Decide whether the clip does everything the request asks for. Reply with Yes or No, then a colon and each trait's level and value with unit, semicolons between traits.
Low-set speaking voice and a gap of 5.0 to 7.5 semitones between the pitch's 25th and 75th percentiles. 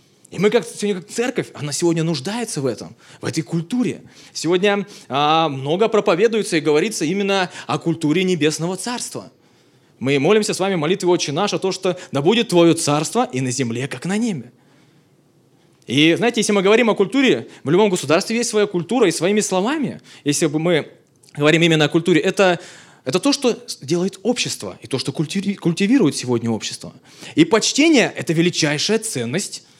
No: medium, 175 Hz; wide, 5.4 semitones